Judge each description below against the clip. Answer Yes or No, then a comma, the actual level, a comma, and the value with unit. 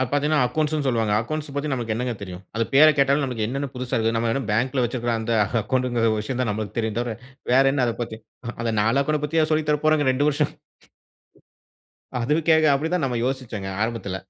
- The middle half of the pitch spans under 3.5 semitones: No, average, 4.0 semitones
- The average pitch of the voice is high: No, low, 125 Hz